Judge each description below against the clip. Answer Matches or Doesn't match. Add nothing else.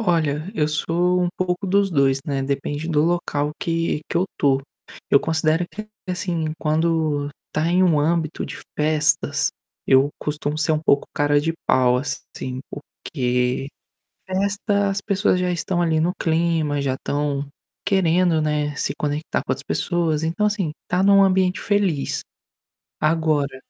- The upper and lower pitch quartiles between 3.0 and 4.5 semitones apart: Matches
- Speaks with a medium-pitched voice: Matches